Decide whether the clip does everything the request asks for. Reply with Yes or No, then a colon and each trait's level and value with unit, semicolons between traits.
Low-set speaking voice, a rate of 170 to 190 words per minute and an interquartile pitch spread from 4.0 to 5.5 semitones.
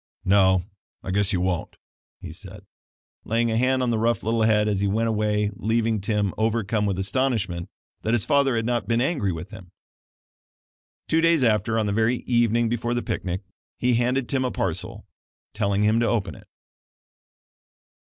No: low, 110 Hz; average, 175 wpm; average, 2.7 semitones